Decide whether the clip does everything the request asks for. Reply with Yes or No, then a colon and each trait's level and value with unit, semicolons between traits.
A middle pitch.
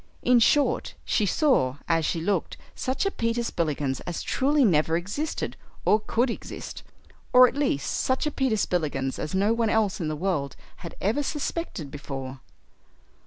No: high, 200 Hz